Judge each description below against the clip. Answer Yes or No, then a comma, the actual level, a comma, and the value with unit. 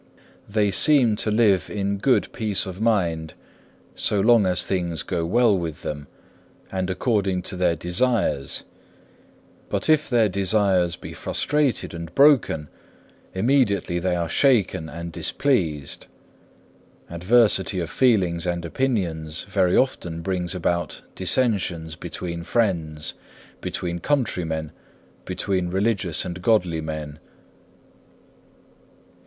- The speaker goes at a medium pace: No, slow, 115 wpm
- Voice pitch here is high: No, very low, 95 Hz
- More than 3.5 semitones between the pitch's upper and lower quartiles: Yes, average, 4.5 semitones